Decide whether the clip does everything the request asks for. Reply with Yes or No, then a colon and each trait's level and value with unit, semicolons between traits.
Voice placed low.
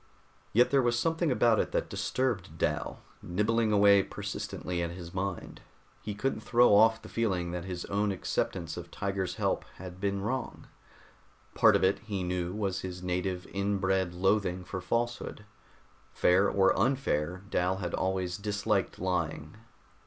Yes: very low, 95 Hz